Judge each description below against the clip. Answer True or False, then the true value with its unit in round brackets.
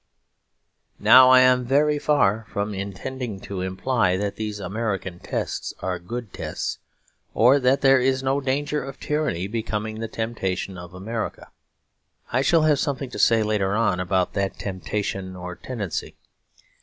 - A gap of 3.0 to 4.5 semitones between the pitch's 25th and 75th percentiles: False (5.3 semitones)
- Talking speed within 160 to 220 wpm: False (150 wpm)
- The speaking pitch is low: True (110 Hz)